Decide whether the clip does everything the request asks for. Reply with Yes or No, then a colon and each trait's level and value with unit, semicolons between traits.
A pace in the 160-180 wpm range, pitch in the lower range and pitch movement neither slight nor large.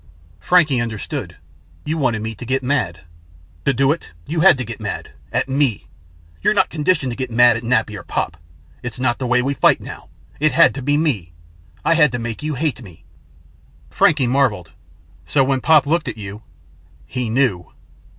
No: average, 190 wpm; low, 130 Hz; average, 4.3 semitones